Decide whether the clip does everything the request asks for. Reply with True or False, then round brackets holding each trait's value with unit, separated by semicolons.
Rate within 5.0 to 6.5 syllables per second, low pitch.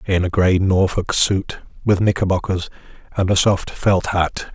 False (4.2 syllables/s; 95 Hz)